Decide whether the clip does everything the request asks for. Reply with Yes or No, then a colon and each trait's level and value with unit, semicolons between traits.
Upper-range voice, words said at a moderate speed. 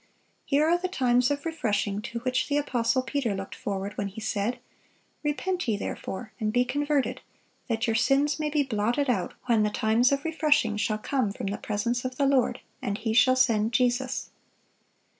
Yes: high, 245 Hz; average, 185 wpm